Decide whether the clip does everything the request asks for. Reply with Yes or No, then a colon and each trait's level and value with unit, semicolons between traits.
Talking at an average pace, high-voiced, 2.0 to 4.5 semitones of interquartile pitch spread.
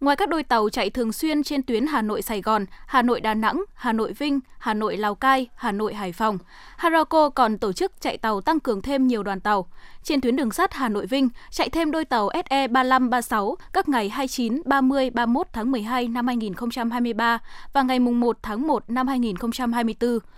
Yes: average, 205 wpm; high, 245 Hz; average, 3.7 semitones